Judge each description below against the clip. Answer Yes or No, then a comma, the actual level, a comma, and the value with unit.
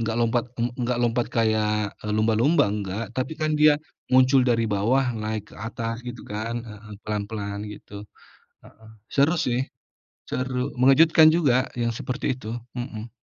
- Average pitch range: Yes, average, 3.0 semitones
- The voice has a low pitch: Yes, low, 115 Hz